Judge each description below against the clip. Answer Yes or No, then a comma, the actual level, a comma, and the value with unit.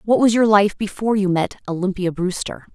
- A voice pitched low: No, high, 195 Hz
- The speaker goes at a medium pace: Yes, average, 195 wpm